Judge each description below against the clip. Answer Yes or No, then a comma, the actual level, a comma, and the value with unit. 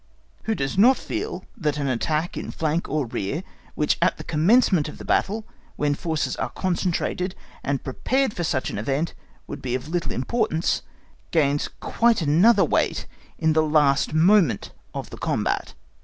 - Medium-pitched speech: Yes, medium, 160 Hz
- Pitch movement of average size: Yes, average, 4.6 semitones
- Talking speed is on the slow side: No, average, 170 wpm